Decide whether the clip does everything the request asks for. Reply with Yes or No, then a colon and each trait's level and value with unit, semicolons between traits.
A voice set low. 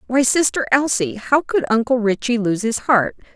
No: high, 235 Hz